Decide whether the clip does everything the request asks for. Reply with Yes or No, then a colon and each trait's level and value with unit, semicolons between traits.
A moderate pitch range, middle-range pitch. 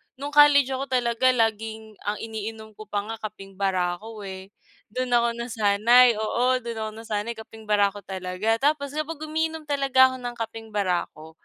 No: average, 3.7 semitones; high, 225 Hz